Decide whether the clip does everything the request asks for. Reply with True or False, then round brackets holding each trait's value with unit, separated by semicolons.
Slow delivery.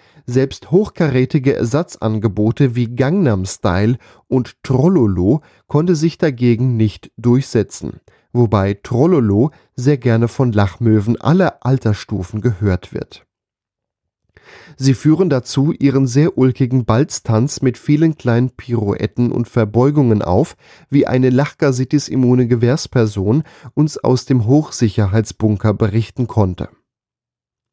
True (100 wpm)